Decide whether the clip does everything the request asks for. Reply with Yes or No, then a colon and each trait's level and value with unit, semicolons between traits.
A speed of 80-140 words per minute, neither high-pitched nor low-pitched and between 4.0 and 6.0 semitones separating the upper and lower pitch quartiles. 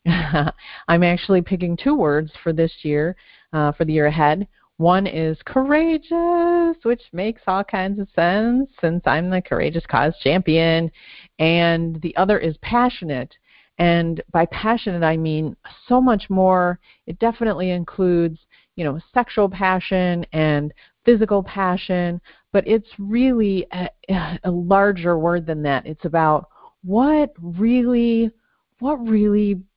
Yes: slow, 135 wpm; medium, 180 Hz; average, 4.4 semitones